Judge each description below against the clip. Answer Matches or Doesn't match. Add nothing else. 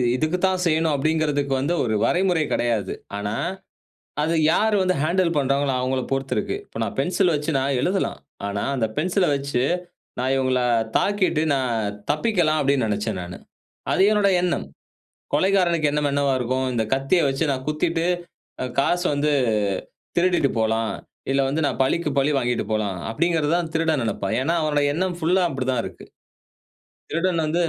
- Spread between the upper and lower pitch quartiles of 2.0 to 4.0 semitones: Doesn't match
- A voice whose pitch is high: Doesn't match